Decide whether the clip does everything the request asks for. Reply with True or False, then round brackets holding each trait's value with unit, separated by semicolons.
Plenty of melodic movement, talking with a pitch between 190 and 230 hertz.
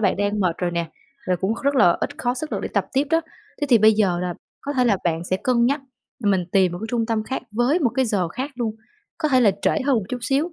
True (5.8 semitones; 225 Hz)